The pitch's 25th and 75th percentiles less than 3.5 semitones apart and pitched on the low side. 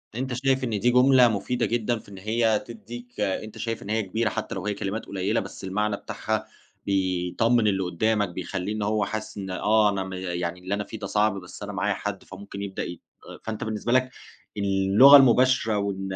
Yes: average, 3.1 semitones; low, 105 Hz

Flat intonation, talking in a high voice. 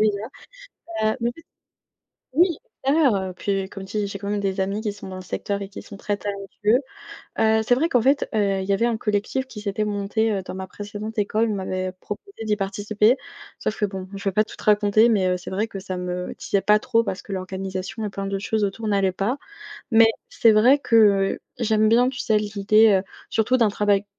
Yes: narrow, 2.1 semitones; high, 205 Hz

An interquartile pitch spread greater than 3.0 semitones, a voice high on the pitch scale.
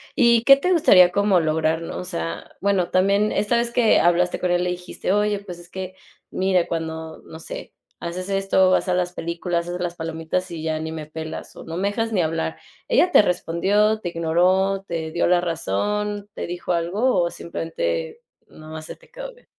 No: average, 3.5 semitones; medium, 180 Hz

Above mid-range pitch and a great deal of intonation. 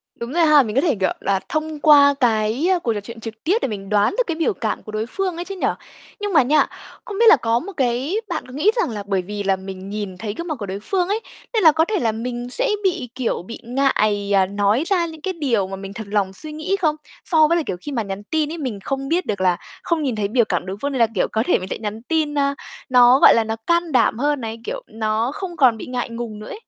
Yes: high, 245 Hz; wide, 6.9 semitones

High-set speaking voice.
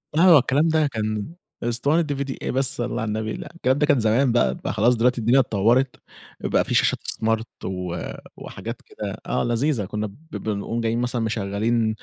No: low, 120 Hz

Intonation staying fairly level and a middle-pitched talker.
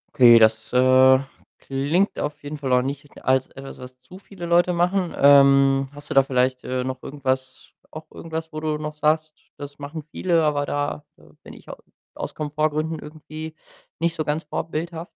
No: average, 3.1 semitones; medium, 145 Hz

